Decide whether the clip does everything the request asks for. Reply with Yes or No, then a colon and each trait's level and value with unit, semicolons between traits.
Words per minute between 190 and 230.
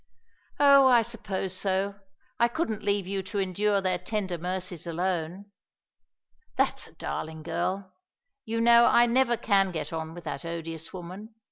No: average, 150 wpm